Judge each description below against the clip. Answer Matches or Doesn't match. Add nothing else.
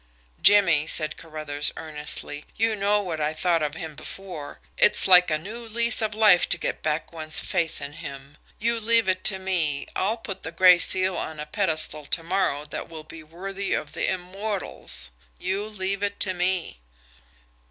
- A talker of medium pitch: Matches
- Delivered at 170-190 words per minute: Matches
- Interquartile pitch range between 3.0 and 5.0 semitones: Matches